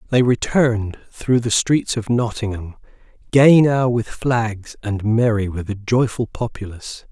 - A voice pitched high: No, low, 115 Hz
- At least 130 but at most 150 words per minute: Yes, average, 145 wpm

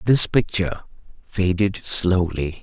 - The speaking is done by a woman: No, male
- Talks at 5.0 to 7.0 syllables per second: No, 3.9 syllables/s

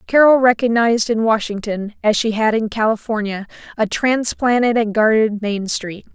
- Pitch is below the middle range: No, high, 220 Hz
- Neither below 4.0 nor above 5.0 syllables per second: Yes, 4.9 syllables/s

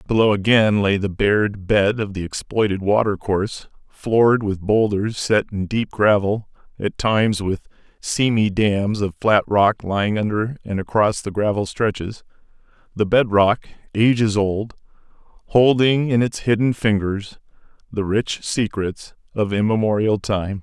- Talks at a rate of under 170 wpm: Yes, average, 145 wpm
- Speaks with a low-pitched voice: Yes, low, 105 Hz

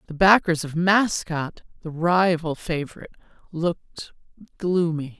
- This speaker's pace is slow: Yes, slow, 105 wpm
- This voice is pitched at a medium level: Yes, medium, 170 Hz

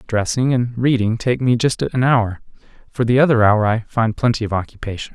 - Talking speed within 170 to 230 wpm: Yes, average, 200 wpm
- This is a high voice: No, low, 115 Hz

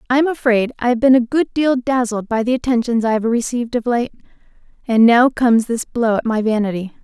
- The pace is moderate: No, fast, 220 wpm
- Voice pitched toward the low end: No, high, 235 Hz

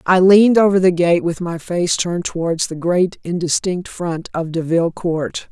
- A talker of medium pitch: Yes, medium, 175 Hz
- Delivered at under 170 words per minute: No, average, 185 wpm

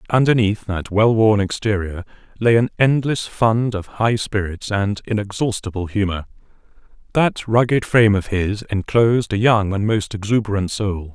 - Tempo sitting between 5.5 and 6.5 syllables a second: No, 4.7 syllables/s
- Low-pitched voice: Yes, low, 105 Hz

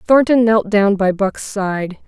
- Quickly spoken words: No, average, 175 wpm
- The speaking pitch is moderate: No, high, 205 Hz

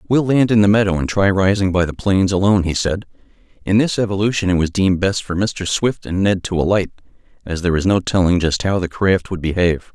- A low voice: Yes, very low, 95 Hz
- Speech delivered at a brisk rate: Yes, fast, 235 wpm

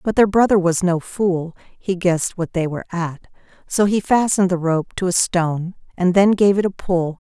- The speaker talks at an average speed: No, fast, 215 wpm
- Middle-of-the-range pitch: Yes, medium, 180 Hz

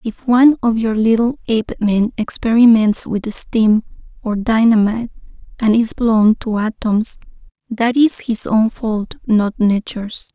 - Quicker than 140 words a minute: No, slow, 135 wpm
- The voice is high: Yes, high, 225 Hz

